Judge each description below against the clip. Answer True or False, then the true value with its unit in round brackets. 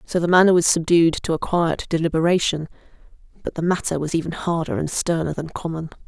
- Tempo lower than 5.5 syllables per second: False (6.0 syllables/s)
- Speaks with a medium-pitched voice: True (165 Hz)